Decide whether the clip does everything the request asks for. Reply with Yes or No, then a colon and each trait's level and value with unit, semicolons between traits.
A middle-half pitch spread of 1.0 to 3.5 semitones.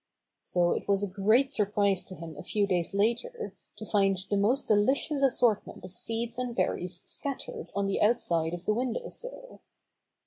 No: average, 4.6 semitones